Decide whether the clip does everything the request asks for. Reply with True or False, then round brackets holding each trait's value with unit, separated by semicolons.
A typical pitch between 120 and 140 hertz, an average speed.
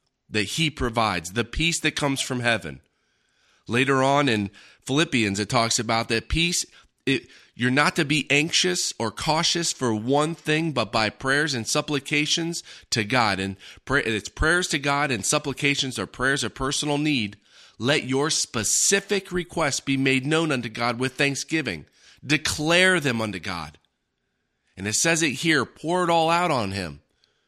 True (135 Hz; 165 wpm)